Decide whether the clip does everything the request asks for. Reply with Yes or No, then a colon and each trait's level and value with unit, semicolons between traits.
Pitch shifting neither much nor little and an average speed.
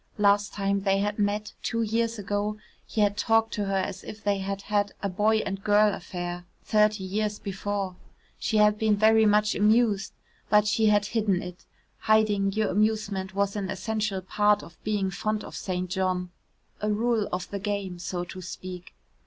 No: narrow, 1.7 semitones; average, 180 wpm